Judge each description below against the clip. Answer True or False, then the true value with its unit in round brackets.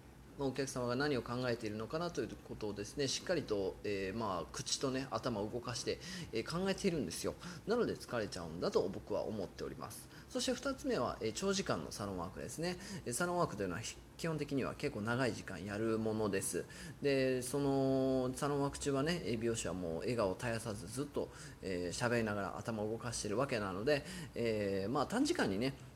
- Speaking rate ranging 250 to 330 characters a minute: False (415 characters per minute)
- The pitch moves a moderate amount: True (5.0 semitones)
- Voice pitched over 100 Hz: True (125 Hz)